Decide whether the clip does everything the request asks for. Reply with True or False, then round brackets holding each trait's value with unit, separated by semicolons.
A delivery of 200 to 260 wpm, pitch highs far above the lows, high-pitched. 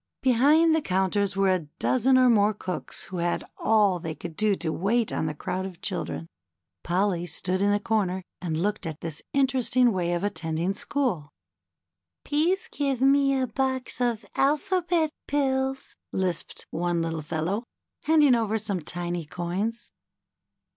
False (155 wpm; 7.0 semitones; 205 Hz)